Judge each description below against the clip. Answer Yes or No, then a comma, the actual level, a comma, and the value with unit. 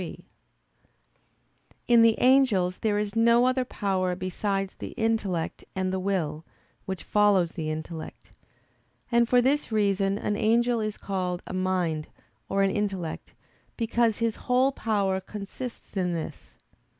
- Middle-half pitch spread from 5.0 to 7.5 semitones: No, average, 3.6 semitones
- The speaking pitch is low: No, high, 200 Hz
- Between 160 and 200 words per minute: No, average, 140 wpm